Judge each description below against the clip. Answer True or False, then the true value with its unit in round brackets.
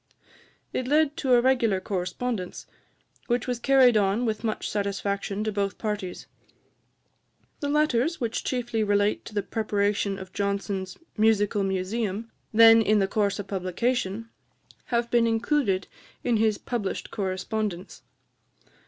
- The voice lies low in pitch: False (215 Hz)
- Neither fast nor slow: False (130 wpm)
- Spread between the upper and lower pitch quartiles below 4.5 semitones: True (3.1 semitones)